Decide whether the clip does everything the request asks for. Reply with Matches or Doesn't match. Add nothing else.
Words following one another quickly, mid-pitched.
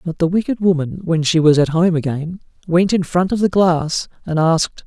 Matches